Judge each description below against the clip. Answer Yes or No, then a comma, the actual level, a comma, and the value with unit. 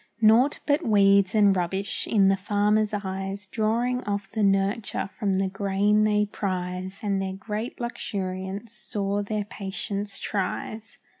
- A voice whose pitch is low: No, high, 200 Hz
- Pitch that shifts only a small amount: Yes, narrow, 1.8 semitones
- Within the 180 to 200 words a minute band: No, average, 140 wpm